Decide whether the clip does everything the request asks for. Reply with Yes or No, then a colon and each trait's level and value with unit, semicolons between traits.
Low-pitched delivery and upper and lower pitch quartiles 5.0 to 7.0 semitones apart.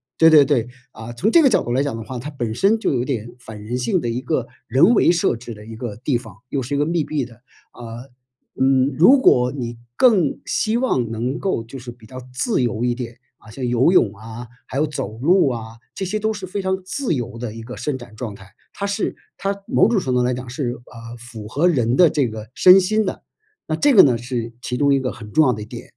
Yes: low, 125 Hz; average, 5.3 semitones